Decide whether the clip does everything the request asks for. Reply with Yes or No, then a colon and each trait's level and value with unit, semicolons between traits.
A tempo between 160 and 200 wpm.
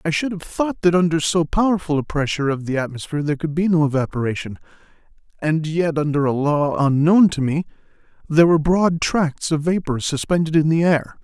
Yes: average, 190 wpm